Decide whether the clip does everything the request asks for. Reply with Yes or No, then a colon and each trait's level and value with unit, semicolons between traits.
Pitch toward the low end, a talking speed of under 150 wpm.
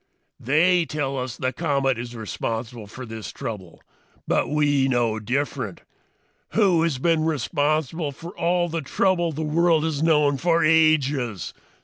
No: medium, 145 Hz; average, 140 wpm